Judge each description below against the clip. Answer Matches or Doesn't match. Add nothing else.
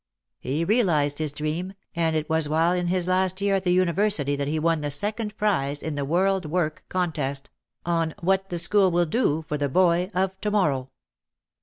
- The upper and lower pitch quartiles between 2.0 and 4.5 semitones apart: Matches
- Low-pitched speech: Doesn't match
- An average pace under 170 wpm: Doesn't match